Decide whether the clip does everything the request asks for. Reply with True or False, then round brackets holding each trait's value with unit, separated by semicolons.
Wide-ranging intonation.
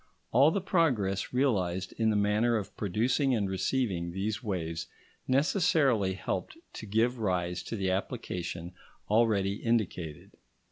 False (4.7 semitones)